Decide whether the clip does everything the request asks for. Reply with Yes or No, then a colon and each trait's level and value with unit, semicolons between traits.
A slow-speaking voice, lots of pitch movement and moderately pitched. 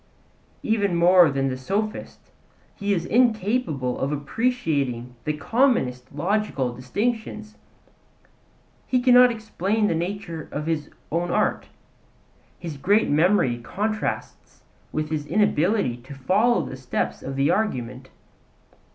Yes: slow, 115 wpm; wide, 7.8 semitones; medium, 170 Hz